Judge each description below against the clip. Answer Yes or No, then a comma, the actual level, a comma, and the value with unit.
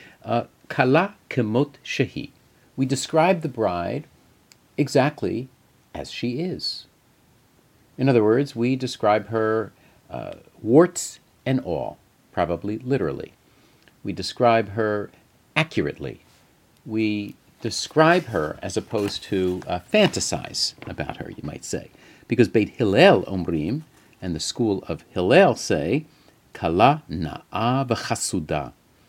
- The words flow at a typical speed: No, slow, 105 wpm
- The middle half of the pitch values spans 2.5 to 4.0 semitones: No, average, 4.9 semitones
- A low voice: Yes, low, 115 Hz